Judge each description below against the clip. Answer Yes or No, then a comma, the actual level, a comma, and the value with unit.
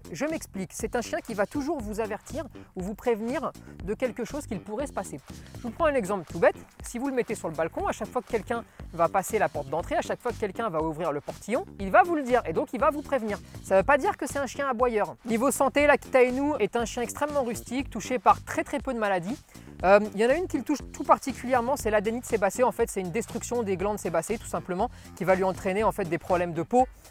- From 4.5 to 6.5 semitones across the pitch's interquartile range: Yes, average, 5.1 semitones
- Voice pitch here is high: Yes, high, 230 Hz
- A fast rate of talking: Yes, fast, 275 wpm